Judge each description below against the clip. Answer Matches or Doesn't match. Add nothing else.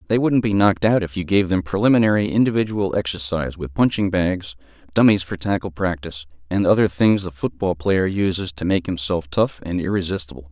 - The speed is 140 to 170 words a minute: Doesn't match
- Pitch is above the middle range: Doesn't match